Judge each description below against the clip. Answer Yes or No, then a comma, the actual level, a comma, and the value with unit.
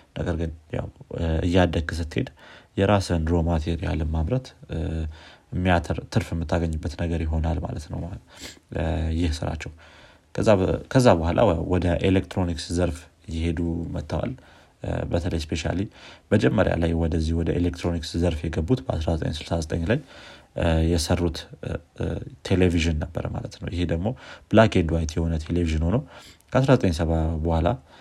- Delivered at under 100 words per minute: No, average, 105 wpm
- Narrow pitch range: Yes, narrow, 2.3 semitones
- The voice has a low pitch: Yes, very low, 85 Hz